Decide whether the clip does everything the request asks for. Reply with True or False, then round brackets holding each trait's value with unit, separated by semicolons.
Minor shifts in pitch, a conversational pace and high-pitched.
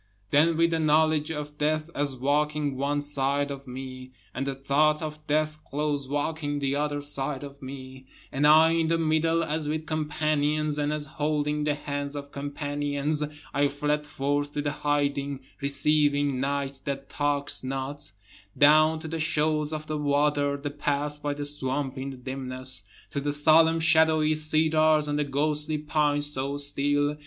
False (1.4 semitones; 165 wpm; 145 Hz)